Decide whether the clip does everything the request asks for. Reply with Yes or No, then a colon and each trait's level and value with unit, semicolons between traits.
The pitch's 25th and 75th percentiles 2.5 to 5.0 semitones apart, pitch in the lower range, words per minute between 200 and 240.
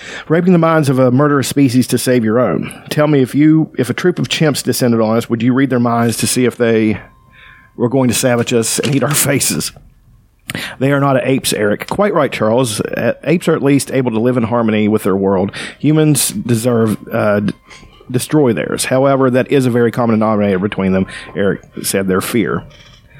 Yes: average, 3.4 semitones; low, 125 Hz; fast, 205 wpm